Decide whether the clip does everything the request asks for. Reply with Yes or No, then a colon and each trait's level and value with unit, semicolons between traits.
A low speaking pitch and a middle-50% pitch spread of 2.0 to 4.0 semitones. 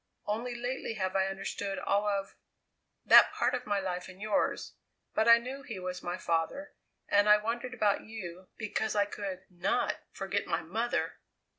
No: high, 205 Hz; average, 3.1 semitones